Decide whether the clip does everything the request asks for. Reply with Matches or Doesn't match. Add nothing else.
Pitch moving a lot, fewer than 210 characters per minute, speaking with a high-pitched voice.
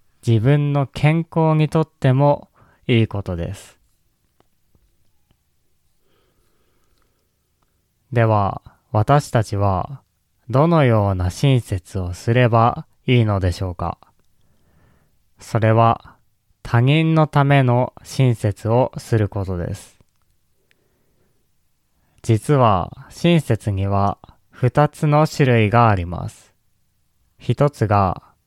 Doesn't match